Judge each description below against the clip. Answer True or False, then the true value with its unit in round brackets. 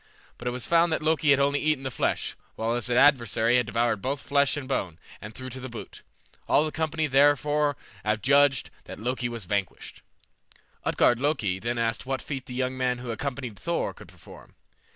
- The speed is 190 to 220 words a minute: True (195 wpm)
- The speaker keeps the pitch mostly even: False (3.4 semitones)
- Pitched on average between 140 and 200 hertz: False (130 Hz)